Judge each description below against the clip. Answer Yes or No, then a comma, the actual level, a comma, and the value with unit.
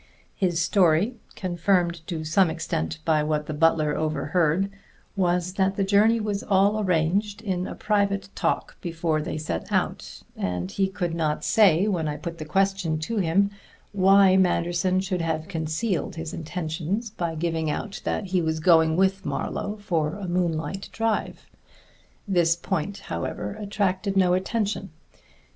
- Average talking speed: Yes, average, 155 wpm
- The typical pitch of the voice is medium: Yes, medium, 180 Hz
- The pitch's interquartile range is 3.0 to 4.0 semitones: Yes, average, 3.5 semitones